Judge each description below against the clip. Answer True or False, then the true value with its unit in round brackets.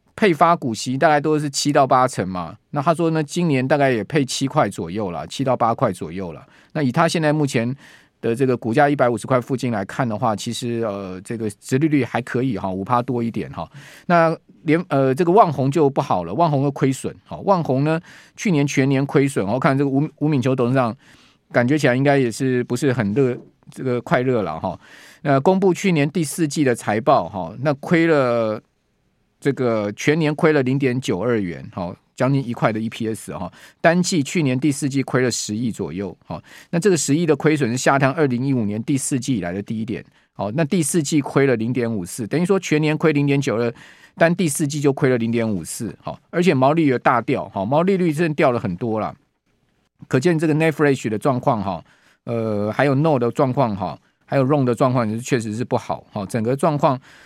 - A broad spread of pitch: False (4.4 semitones)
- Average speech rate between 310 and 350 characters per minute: True (325 characters per minute)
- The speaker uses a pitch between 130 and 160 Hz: True (135 Hz)